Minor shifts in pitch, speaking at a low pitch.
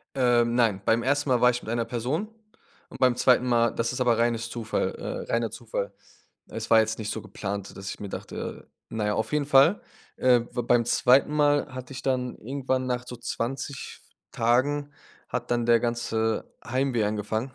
Yes: narrow, 2.2 semitones; low, 120 Hz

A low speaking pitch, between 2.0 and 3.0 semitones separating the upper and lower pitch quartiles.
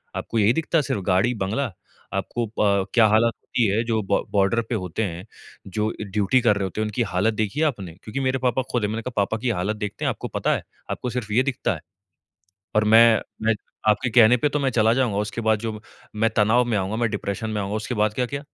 Yes: low, 110 Hz; narrow, 2.6 semitones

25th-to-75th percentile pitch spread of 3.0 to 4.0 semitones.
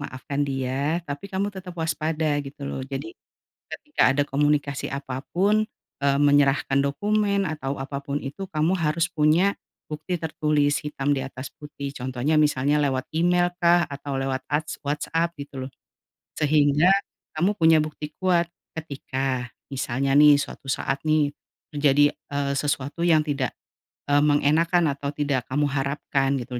No: narrow, 2.6 semitones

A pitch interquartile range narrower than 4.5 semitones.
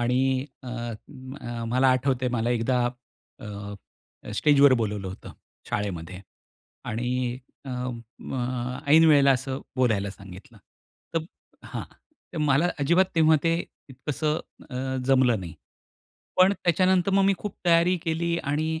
No: average, 4.8 semitones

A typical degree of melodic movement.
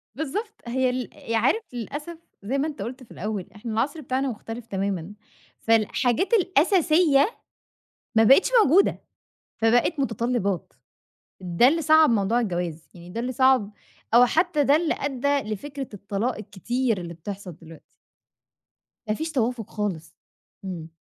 No: wide, 5.7 semitones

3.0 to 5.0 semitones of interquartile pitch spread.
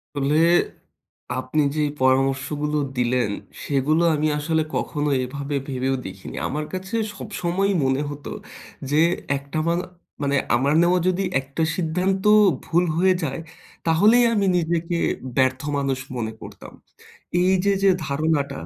Yes: average, 4.2 semitones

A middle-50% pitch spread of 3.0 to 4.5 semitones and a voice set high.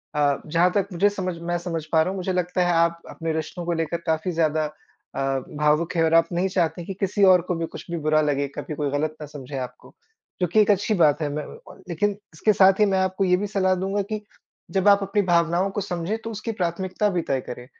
No: average, 3.4 semitones; medium, 175 Hz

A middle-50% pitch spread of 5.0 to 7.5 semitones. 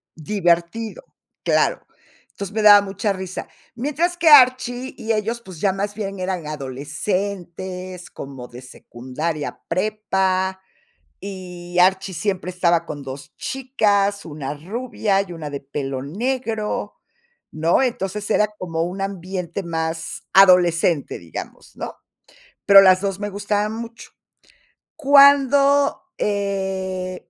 No: average, 3.8 semitones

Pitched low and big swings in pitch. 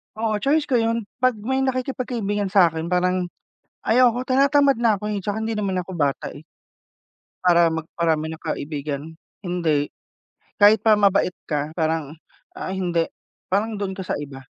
No: high, 195 Hz; wide, 5.7 semitones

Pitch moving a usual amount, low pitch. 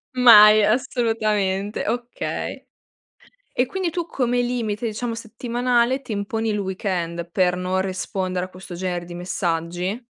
No: average, 4.6 semitones; high, 210 Hz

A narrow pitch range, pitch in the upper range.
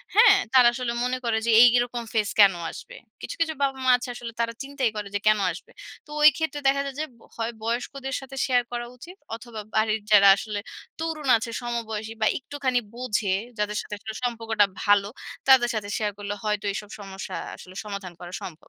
No: average, 3.8 semitones; high, 235 Hz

